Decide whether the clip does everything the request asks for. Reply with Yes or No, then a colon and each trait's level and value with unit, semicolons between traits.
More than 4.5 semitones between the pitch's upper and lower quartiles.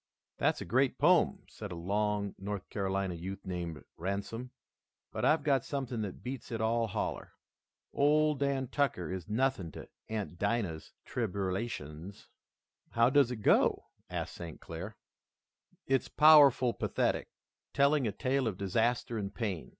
Yes: wide, 5.6 semitones